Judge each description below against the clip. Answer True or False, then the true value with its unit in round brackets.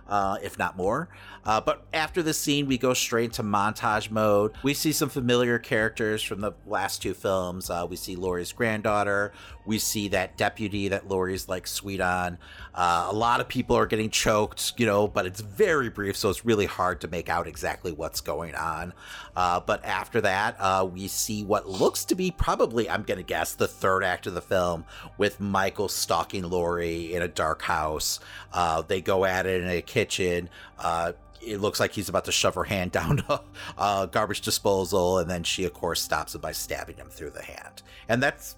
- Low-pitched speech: True (100 Hz)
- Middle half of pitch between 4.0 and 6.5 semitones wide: False (3.1 semitones)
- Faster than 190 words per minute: True (205 wpm)